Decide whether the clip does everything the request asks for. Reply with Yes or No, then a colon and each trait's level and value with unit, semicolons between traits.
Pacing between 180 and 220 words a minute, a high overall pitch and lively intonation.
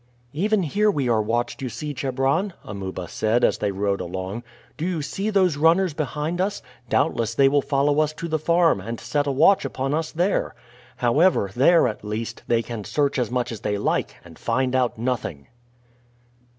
No: average, 190 wpm; low, 135 Hz; wide, 5.8 semitones